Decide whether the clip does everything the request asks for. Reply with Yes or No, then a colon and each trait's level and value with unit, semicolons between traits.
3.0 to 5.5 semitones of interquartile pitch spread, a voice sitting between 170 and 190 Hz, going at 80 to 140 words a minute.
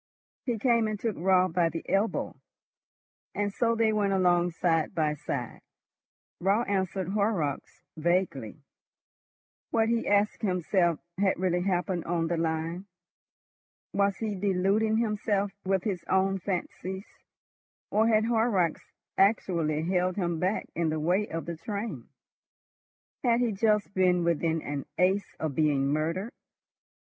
Yes: average, 3.6 semitones; medium, 185 Hz; slow, 135 wpm